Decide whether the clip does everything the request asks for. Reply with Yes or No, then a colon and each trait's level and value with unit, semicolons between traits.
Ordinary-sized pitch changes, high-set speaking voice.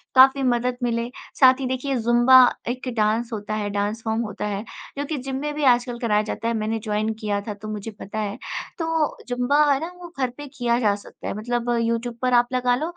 Yes: average, 3.1 semitones; high, 240 Hz